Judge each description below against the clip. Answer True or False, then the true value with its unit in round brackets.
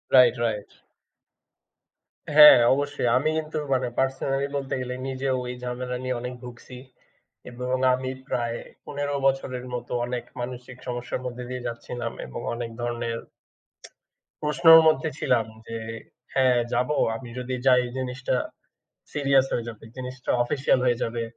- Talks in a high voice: False (125 Hz)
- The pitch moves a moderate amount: False (1.7 semitones)